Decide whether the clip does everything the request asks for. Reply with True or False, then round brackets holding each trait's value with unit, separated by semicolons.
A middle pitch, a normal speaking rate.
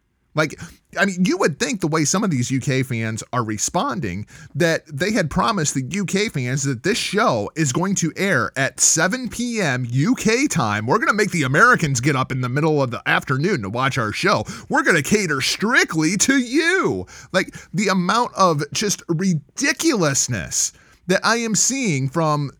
True (170 Hz; 185 wpm)